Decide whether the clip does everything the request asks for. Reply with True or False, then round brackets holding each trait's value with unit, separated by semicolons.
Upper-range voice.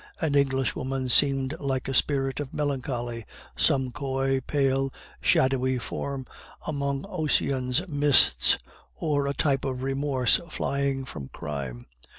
False (135 Hz)